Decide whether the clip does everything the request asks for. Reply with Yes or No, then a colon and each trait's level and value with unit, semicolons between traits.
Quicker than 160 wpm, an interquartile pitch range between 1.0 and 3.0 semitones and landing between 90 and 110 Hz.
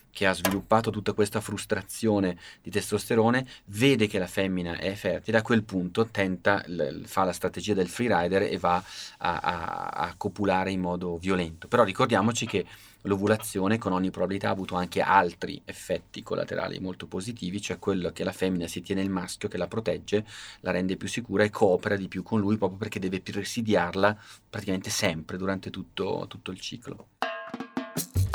Yes: fast, 170 wpm; narrow, 2.4 semitones; low, 100 Hz